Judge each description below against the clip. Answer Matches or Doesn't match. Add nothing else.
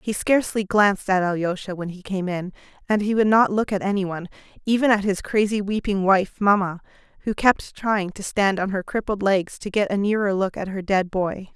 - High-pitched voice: Matches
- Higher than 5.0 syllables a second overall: Matches